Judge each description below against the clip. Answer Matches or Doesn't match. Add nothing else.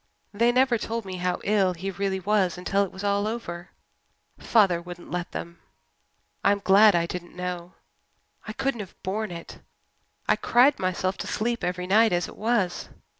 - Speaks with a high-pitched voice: Matches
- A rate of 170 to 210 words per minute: Matches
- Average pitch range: Matches